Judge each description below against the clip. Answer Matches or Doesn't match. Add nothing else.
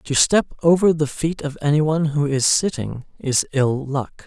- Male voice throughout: Matches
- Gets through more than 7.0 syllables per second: Doesn't match